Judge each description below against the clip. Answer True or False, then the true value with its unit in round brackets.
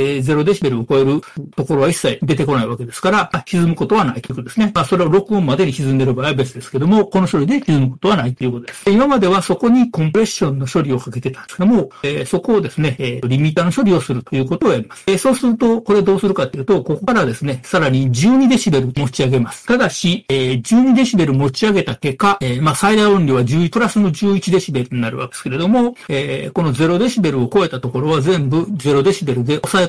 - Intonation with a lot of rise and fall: True (6.8 semitones)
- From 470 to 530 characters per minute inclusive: True (480 characters per minute)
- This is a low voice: False (165 Hz)